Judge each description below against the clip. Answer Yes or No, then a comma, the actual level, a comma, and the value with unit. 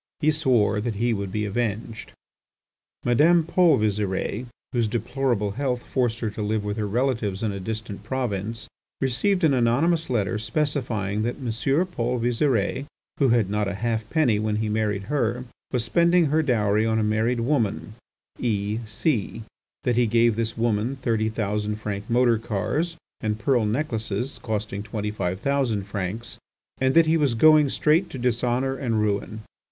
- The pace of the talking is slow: No, average, 165 wpm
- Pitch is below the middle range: Yes, low, 115 Hz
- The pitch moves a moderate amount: Yes, average, 3.8 semitones